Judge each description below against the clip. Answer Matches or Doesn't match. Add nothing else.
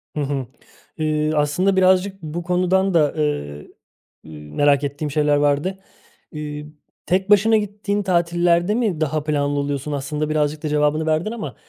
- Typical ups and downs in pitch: Matches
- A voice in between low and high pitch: Matches